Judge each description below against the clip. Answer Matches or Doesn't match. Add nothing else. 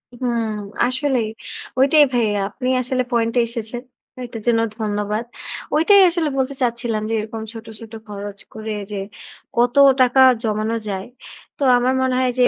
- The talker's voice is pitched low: Doesn't match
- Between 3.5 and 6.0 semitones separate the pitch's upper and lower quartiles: Doesn't match